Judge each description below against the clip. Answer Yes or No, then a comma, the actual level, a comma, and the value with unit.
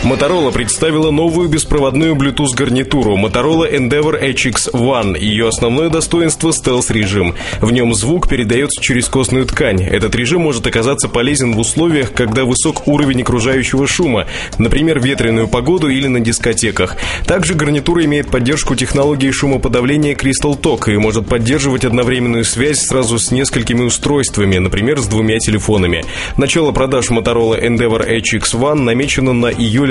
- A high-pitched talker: No, low, 130 Hz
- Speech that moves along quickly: No, average, 140 wpm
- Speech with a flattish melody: No, average, 3.9 semitones